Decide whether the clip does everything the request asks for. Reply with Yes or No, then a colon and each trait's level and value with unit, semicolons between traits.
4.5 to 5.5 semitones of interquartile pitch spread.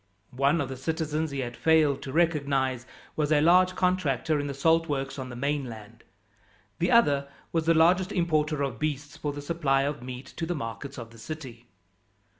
No: average, 3.3 semitones